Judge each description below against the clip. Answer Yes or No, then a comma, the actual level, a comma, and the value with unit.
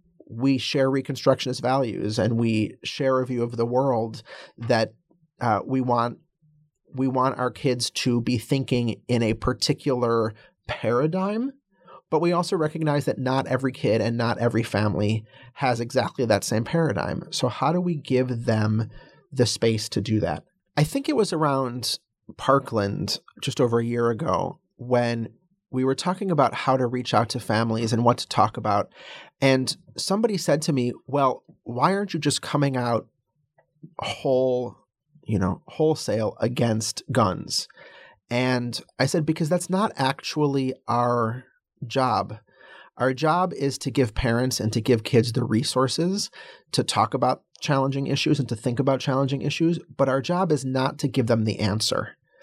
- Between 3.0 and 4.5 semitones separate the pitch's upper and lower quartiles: Yes, average, 4.0 semitones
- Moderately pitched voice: No, low, 130 Hz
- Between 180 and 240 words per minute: No, average, 160 wpm